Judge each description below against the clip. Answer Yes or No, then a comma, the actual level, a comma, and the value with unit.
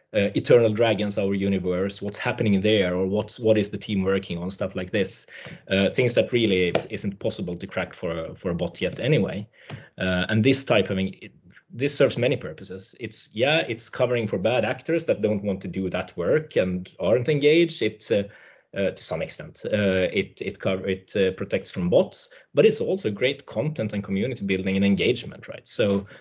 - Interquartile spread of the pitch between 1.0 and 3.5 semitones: Yes, narrow, 2.5 semitones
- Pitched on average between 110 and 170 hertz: No, low, 100 Hz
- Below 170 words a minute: No, average, 200 wpm